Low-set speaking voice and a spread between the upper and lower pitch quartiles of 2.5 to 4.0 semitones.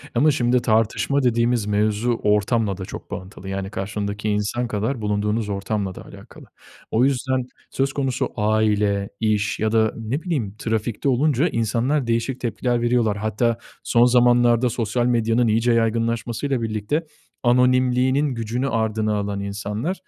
Yes: low, 115 Hz; average, 2.8 semitones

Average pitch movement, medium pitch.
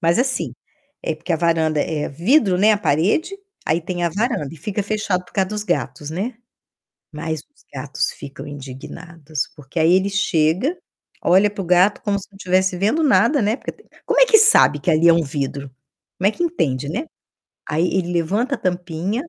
Yes: average, 4.9 semitones; medium, 180 Hz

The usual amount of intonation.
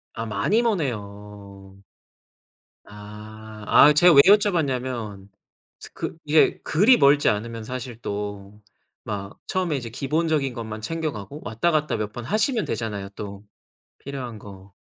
No: wide, 6.5 semitones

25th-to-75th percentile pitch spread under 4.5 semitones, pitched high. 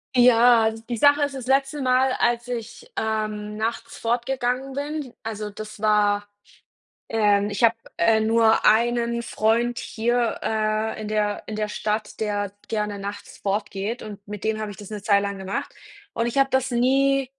Yes: narrow, 2.6 semitones; high, 225 Hz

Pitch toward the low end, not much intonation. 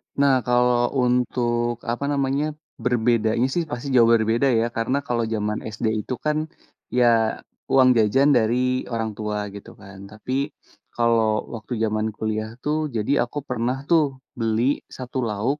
No: low, 120 Hz; average, 3.2 semitones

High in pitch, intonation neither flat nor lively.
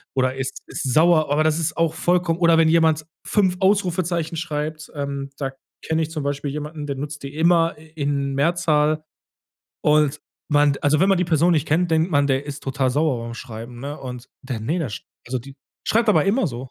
No: medium, 150 Hz; average, 3.1 semitones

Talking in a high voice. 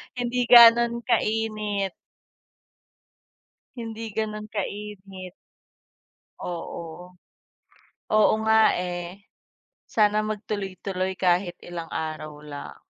Yes: high, 205 Hz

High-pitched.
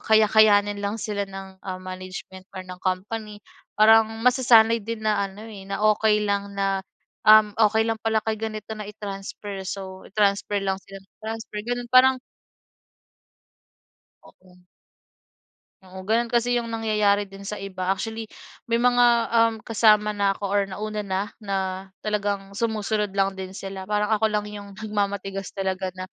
Yes: high, 205 Hz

